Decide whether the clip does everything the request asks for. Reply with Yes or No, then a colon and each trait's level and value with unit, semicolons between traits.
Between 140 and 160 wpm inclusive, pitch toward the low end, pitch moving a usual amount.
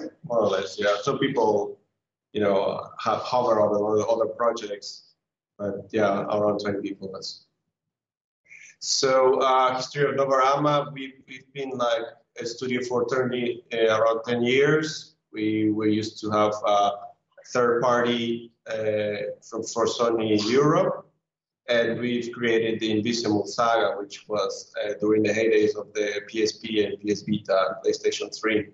Yes: average, 155 wpm; low, 120 Hz; average, 3.9 semitones